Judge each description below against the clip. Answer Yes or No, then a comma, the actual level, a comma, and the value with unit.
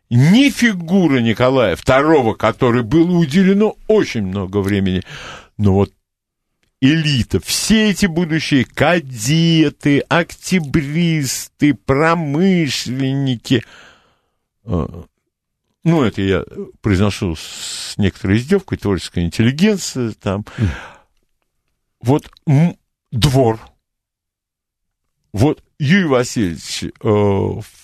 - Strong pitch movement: Yes, wide, 8.2 semitones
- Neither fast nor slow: No, slow, 75 wpm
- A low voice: Yes, low, 130 Hz